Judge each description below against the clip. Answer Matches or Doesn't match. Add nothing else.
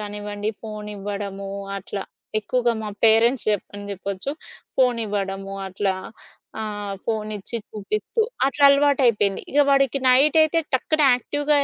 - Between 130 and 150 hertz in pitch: Doesn't match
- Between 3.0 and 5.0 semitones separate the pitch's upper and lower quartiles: Matches